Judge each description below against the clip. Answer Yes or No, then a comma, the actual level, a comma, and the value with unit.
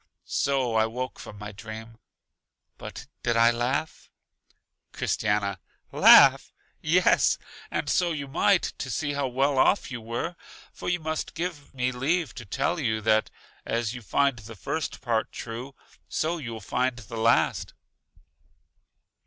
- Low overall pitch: Yes, low, 125 Hz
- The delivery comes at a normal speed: Yes, average, 150 wpm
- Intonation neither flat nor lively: Yes, average, 4.4 semitones